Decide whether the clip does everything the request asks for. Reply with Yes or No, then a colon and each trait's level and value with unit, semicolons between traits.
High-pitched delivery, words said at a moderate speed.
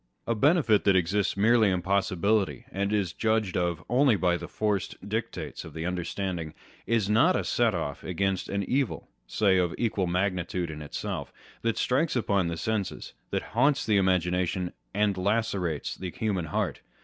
No: low, 100 Hz; average, 165 wpm